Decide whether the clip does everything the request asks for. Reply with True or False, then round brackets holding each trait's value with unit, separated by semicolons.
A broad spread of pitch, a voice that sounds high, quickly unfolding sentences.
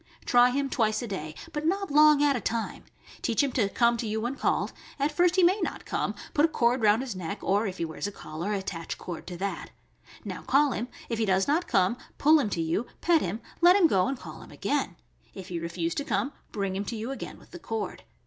True (6.7 semitones; 230 Hz; 245 wpm)